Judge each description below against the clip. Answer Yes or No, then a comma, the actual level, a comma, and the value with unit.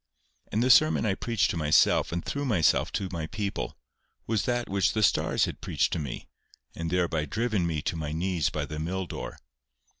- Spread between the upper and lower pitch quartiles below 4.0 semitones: No, average, 5.2 semitones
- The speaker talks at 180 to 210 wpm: Yes, average, 200 wpm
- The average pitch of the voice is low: Yes, very low, 90 Hz